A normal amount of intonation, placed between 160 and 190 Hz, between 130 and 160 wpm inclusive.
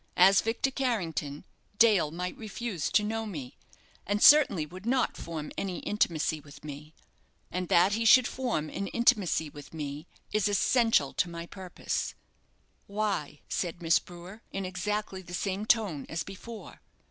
Yes: average, 5.0 semitones; medium, 185 Hz; average, 150 wpm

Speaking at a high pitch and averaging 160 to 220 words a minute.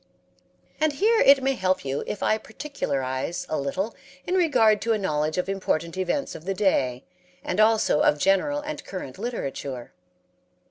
Yes: high, 195 Hz; average, 165 wpm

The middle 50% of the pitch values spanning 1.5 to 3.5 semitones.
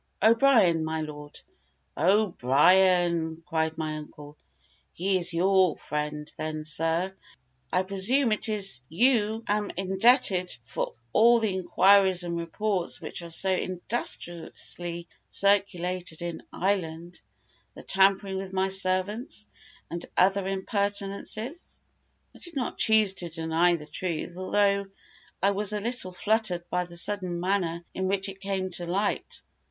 Yes: average, 2.9 semitones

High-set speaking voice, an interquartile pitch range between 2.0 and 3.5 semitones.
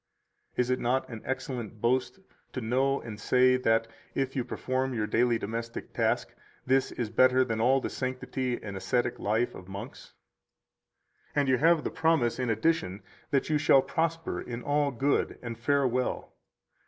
No: low, 125 Hz; average, 2.7 semitones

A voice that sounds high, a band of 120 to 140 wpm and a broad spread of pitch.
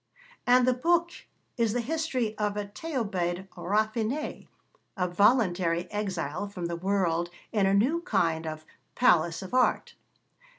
Yes: high, 205 Hz; slow, 135 wpm; wide, 5.8 semitones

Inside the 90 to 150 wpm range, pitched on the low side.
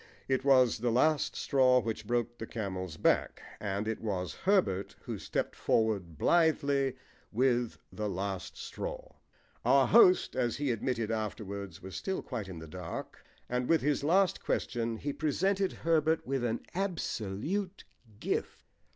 Yes: average, 145 wpm; low, 120 Hz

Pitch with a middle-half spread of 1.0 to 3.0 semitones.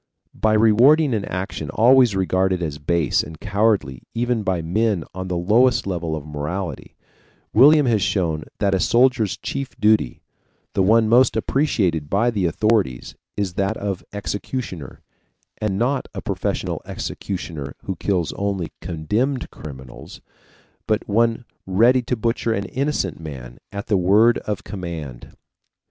No: average, 5.1 semitones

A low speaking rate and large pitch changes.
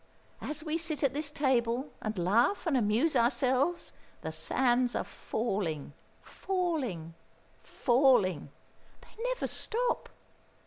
Yes: slow, 110 wpm; wide, 5.8 semitones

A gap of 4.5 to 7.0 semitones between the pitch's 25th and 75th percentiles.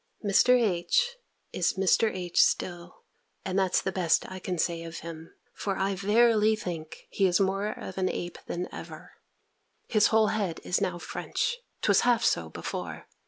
No: average, 3.5 semitones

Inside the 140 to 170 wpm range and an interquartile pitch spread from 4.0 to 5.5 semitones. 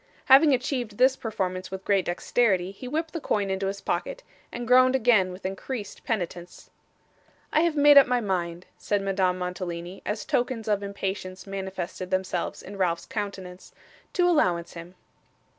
Yes: average, 160 wpm; average, 5.1 semitones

